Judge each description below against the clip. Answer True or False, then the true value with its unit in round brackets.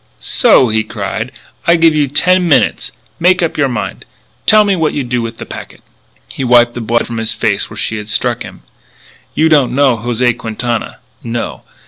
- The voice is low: True (125 Hz)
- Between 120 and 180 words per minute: False (190 wpm)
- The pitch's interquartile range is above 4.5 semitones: True (5.2 semitones)